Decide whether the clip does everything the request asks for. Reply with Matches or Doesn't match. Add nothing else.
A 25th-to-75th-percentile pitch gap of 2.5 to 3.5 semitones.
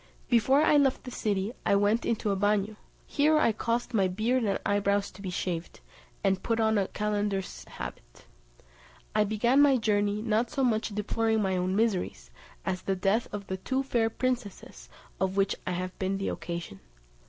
Matches